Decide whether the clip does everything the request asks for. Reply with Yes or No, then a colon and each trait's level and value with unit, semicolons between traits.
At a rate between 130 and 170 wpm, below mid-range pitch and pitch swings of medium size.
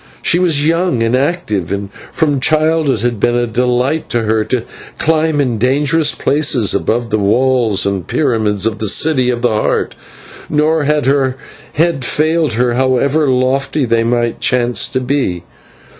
Yes: average, 165 wpm; low, 130 Hz; average, 4.6 semitones